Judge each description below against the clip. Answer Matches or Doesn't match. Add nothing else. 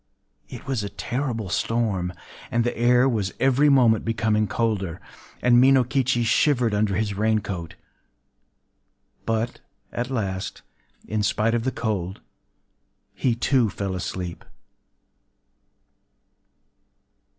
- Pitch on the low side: Matches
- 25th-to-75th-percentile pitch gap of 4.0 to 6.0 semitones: Doesn't match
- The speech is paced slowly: Matches